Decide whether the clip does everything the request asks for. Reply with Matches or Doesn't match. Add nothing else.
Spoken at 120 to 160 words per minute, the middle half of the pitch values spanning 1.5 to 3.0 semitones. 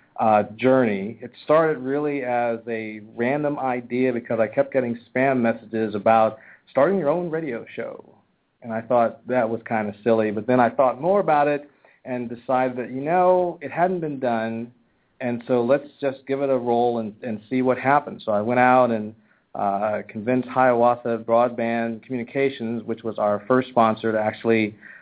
Doesn't match